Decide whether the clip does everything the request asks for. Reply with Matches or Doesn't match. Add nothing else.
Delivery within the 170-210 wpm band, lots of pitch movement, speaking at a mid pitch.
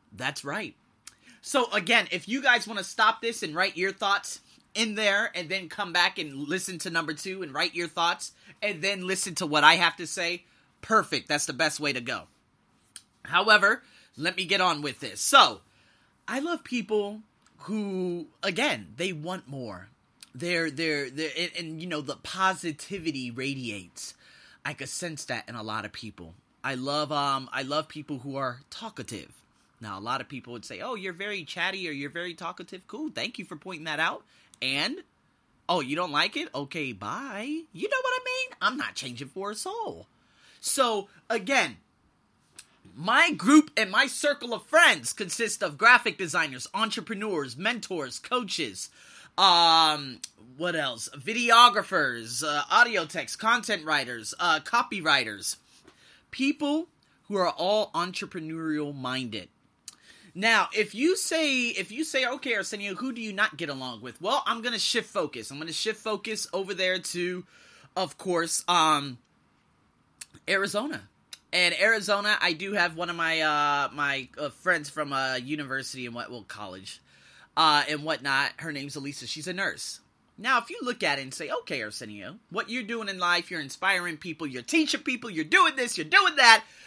Matches